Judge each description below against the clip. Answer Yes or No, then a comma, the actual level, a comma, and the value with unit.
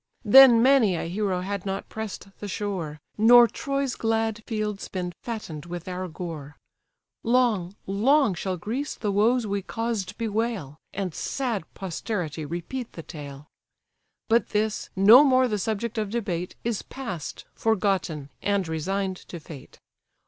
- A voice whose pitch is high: Yes, high, 200 Hz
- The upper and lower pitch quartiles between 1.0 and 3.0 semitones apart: No, average, 4.3 semitones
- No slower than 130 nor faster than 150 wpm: Yes, average, 140 wpm